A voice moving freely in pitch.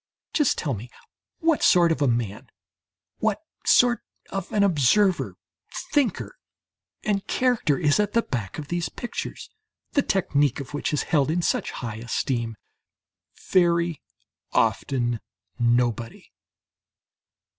Yes: wide, 8.3 semitones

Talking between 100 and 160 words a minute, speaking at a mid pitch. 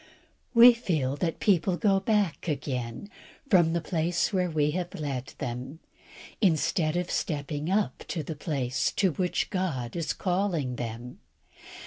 Yes: average, 140 wpm; medium, 165 Hz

